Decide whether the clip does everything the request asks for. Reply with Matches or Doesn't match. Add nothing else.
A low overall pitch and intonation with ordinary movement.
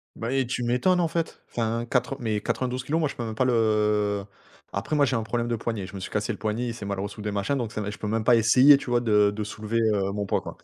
Matches